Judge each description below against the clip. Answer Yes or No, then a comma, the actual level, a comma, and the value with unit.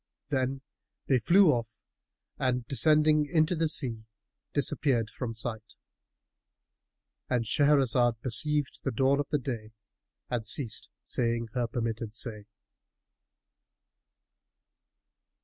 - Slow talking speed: Yes, slow, 95 wpm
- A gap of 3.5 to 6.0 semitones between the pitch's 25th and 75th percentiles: Yes, average, 3.9 semitones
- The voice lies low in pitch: Yes, low, 125 Hz